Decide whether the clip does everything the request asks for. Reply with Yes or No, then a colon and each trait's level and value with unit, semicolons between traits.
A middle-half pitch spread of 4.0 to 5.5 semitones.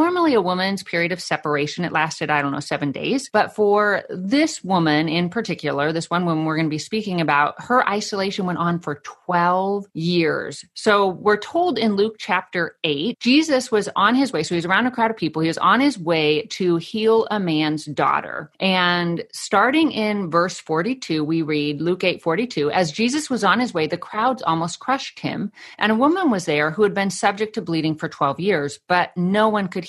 Yes: average, 5.0 semitones